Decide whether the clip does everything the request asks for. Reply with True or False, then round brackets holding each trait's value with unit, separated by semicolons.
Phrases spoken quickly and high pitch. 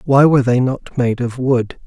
False (225 wpm; 125 Hz)